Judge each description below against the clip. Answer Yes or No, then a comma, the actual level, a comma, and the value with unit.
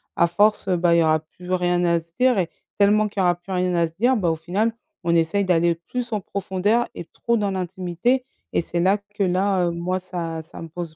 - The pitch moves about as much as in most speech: Yes, average, 3.0 semitones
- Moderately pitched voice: Yes, medium, 180 Hz